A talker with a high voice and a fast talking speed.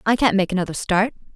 Yes: high, 200 Hz; fast, 220 wpm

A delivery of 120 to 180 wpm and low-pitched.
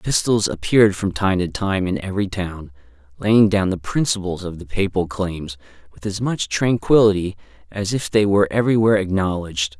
Yes: average, 165 wpm; very low, 95 Hz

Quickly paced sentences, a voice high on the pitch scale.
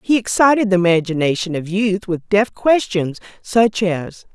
No: average, 150 wpm; high, 195 Hz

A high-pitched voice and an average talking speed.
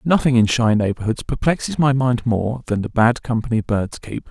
No: low, 115 Hz; average, 195 wpm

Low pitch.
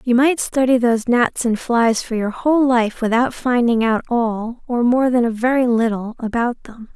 No: high, 240 Hz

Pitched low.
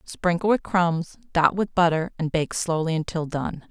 No: medium, 170 Hz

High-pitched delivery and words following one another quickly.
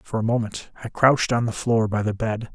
No: low, 115 Hz; fast, 260 wpm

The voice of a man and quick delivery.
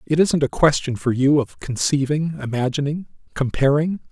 No: male; average, 145 wpm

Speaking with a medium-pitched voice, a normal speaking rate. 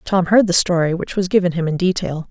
No: medium, 175 Hz; fast, 260 wpm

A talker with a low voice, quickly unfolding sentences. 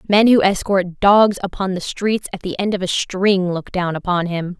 No: high, 190 Hz; fast, 220 wpm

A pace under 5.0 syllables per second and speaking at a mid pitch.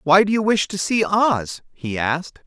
Yes: 4.5 syllables/s; medium, 180 Hz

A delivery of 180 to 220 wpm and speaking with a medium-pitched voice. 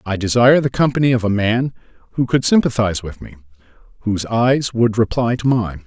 No: average, 185 wpm; low, 115 Hz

